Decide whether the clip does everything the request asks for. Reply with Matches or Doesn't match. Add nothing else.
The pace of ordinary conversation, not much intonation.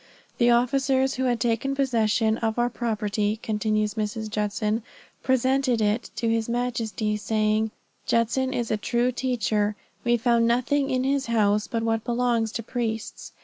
Matches